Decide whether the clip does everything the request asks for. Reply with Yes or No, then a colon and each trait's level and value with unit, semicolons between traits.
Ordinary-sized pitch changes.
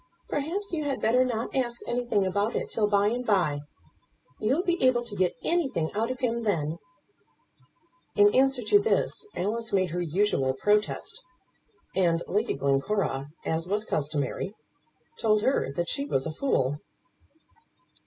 No: wide, 6.6 semitones